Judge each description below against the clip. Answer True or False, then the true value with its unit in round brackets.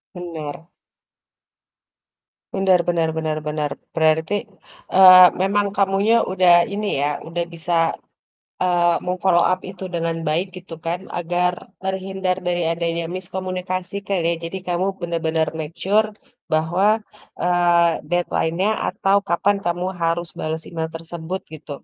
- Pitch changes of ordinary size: False (2.1 semitones)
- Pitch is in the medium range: True (175 Hz)